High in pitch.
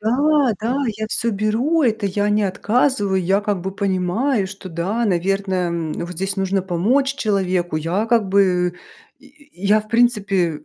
Yes: high, 200 Hz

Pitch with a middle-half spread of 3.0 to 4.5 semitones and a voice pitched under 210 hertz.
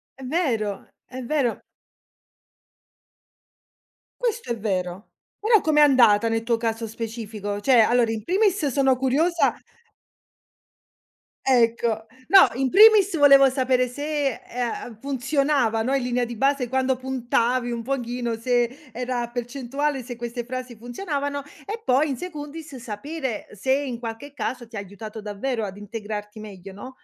No: average, 3.5 semitones; very high, 250 Hz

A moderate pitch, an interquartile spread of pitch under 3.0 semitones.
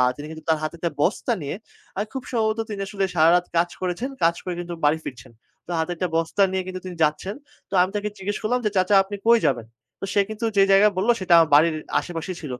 No: medium, 180 Hz; average, 4.0 semitones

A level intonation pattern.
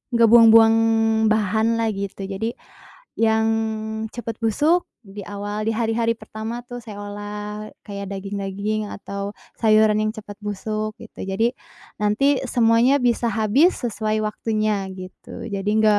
Yes: narrow, 1.8 semitones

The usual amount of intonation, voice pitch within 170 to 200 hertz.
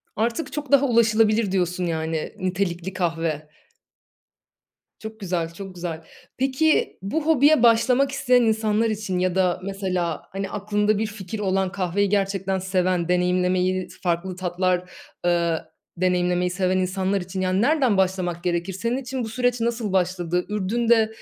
Yes: average, 3.7 semitones; high, 190 Hz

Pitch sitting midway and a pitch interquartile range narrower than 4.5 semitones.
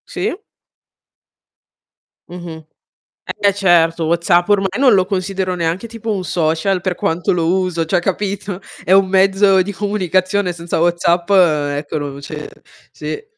Yes: medium, 180 Hz; narrow, 2.6 semitones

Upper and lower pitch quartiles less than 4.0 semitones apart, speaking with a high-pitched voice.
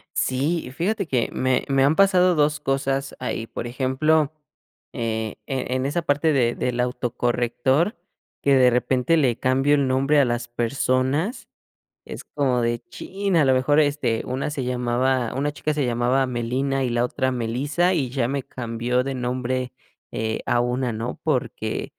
No: average, 2.9 semitones; low, 130 Hz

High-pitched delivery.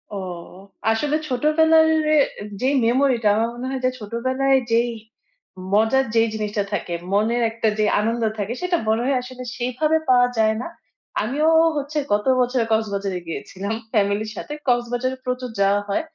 Yes: high, 240 Hz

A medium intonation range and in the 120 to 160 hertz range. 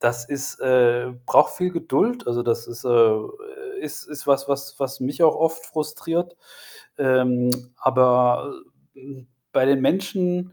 Yes: average, 4.6 semitones; low, 135 Hz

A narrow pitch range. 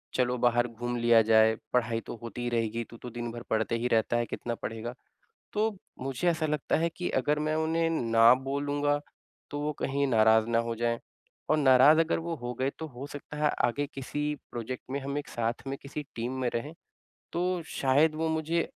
No: average, 4.2 semitones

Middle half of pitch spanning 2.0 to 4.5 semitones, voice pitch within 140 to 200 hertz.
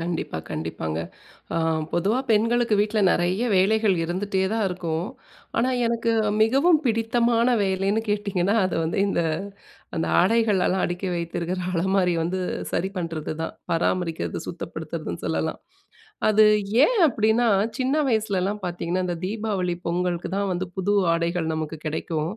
Yes: average, 4.0 semitones; high, 190 Hz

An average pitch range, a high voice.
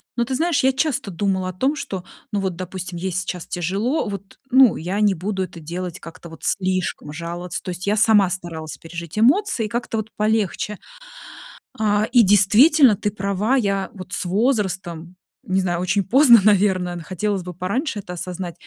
Yes: average, 3.4 semitones; high, 195 Hz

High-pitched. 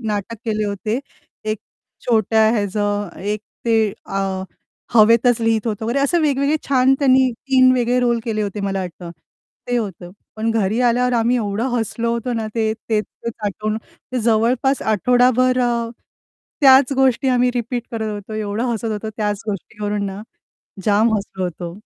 Yes: high, 225 Hz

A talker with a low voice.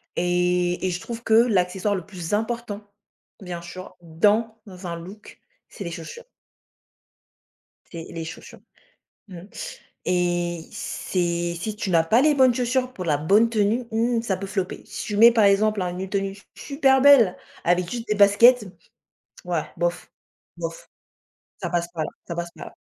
No: high, 190 Hz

